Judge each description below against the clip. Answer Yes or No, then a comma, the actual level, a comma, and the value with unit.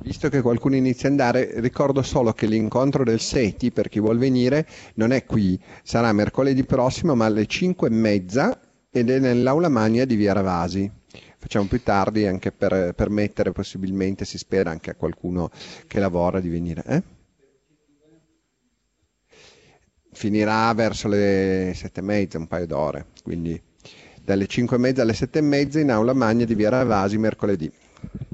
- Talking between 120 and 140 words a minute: No, average, 160 wpm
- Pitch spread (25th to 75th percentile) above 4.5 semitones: Yes, average, 4.9 semitones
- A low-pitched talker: Yes, low, 110 Hz